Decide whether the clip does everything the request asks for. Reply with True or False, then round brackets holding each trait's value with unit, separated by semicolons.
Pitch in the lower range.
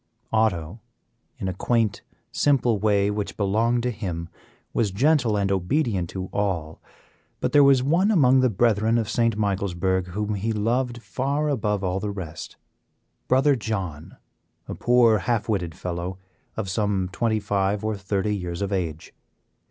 True (105 Hz)